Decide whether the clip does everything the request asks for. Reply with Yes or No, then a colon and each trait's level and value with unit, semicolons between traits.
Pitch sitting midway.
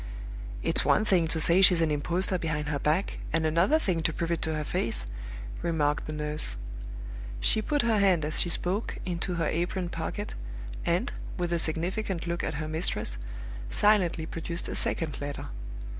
Yes: medium, 170 Hz